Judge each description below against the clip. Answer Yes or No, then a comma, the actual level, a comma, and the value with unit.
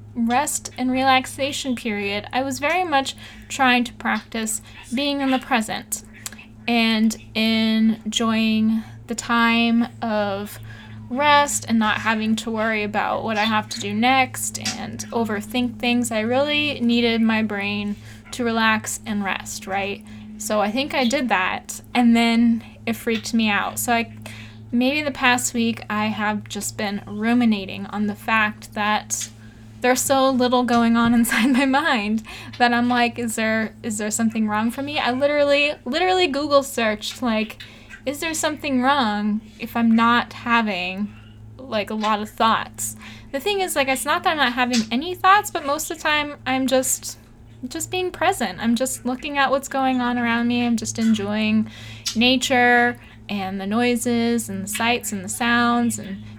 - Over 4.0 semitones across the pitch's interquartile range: No, average, 3.7 semitones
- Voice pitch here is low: No, high, 230 Hz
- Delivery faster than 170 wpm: No, average, 165 wpm